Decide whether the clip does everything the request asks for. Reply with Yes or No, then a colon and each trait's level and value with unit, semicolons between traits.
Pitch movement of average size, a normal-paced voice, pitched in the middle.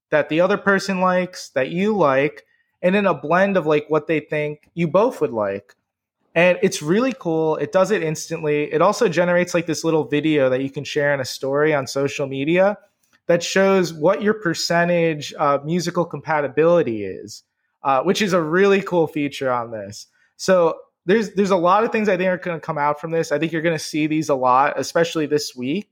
No: average, 3.8 semitones; fast, 215 wpm; medium, 165 Hz